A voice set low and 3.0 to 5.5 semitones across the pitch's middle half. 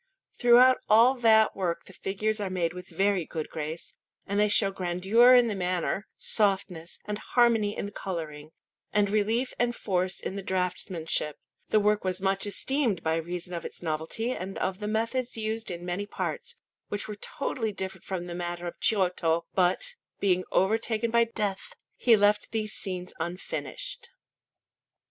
No: high, 195 Hz; average, 3.5 semitones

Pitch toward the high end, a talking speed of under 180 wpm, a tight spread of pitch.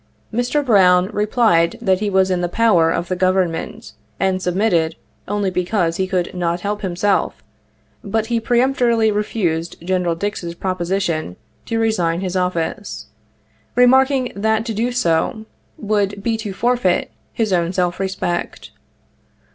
No: high, 195 Hz; average, 140 wpm; average, 3.9 semitones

